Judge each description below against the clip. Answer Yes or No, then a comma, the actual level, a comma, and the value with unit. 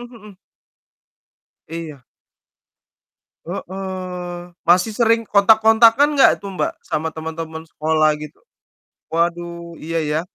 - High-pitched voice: No, medium, 175 Hz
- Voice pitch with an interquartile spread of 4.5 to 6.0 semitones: No, average, 3.9 semitones